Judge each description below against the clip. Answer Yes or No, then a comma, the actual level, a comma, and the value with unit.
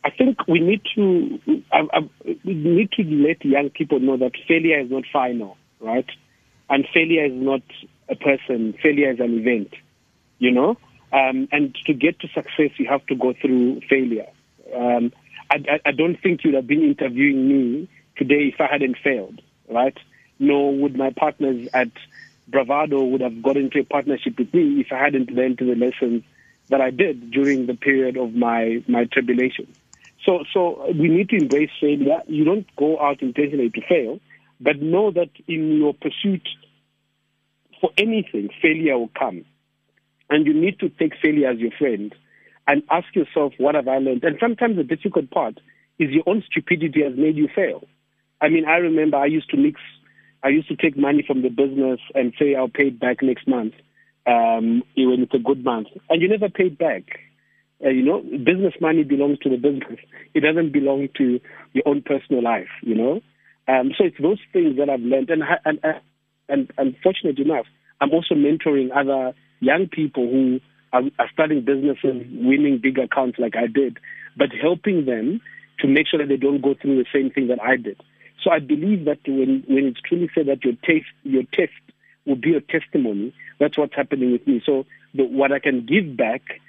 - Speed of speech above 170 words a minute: Yes, average, 190 wpm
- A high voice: No, medium, 140 Hz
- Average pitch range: Yes, average, 3.8 semitones